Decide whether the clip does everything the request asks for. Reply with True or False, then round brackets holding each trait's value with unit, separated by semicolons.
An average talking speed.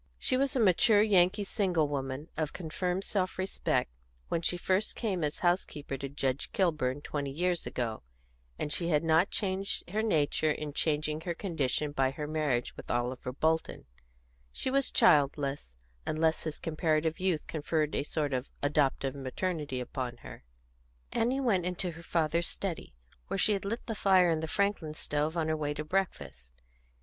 True (170 wpm)